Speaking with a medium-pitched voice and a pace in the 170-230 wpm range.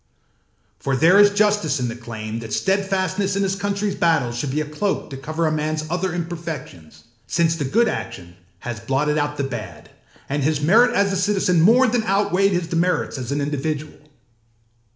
Yes: medium, 160 Hz; average, 190 wpm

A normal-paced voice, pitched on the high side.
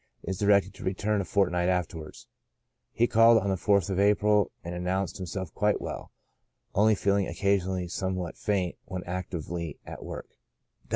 No: average, 155 wpm; very low, 95 Hz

